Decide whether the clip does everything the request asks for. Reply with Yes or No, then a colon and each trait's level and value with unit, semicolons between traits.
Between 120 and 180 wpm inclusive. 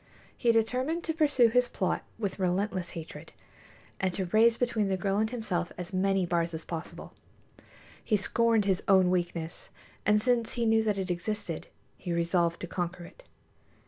Yes: average, 170 wpm